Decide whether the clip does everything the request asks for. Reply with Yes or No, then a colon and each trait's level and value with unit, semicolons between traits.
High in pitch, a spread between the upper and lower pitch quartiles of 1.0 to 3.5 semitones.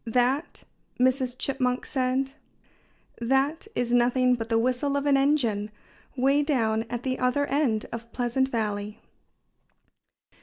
Yes: very high, 250 Hz; narrow, 2.5 semitones